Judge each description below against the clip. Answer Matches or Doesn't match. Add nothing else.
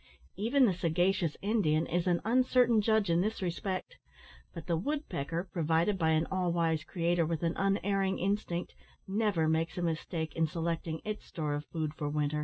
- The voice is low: Doesn't match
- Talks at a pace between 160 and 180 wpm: Matches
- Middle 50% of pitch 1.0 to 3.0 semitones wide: Doesn't match